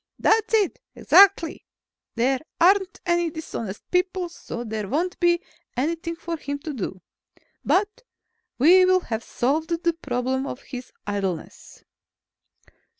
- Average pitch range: No, wide, 6.4 semitones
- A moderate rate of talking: No, slow, 125 wpm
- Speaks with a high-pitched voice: Yes, very high, 325 Hz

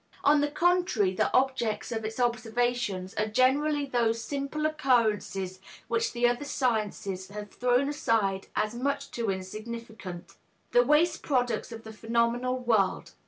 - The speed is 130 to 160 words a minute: Yes, average, 140 wpm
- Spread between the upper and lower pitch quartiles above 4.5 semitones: No, average, 3.7 semitones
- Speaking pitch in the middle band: No, high, 235 Hz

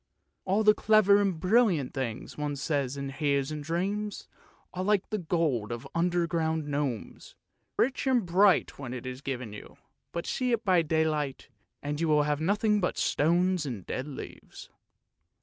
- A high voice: No, medium, 160 Hz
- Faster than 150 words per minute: Yes, average, 165 wpm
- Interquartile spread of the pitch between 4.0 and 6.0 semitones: Yes, wide, 5.5 semitones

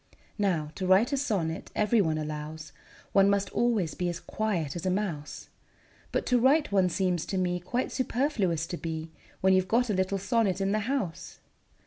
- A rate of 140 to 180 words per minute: No, average, 190 wpm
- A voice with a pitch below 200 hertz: Yes, high, 190 Hz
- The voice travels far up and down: No, average, 4.4 semitones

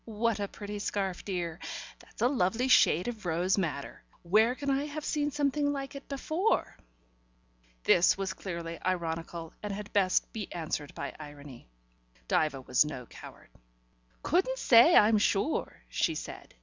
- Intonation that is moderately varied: No, wide, 7.5 semitones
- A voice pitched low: No, high, 200 Hz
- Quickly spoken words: No, average, 150 wpm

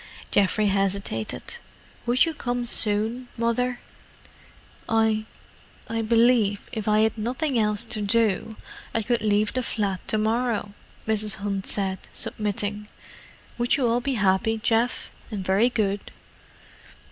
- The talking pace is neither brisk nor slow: No, slow, 125 wpm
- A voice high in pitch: Yes, high, 220 Hz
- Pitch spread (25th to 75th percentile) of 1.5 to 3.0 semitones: Yes, narrow, 2.5 semitones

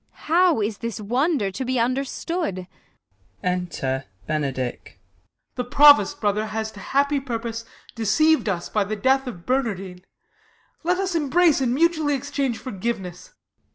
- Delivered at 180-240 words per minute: No, average, 140 wpm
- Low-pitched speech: No, high, 235 Hz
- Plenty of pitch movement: Yes, wide, 6.1 semitones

